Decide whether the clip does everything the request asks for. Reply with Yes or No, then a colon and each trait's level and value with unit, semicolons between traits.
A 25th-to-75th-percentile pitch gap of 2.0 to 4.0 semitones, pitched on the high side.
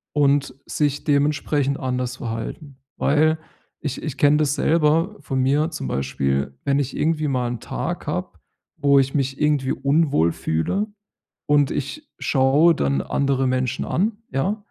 No: average, 2.7 semitones; medium, 140 Hz